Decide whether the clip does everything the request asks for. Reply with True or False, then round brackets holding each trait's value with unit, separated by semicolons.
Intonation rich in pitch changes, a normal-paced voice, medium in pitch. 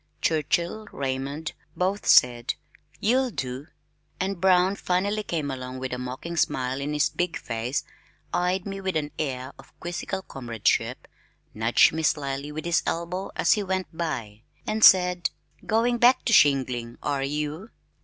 True (6.1 semitones; 150 wpm; 160 Hz)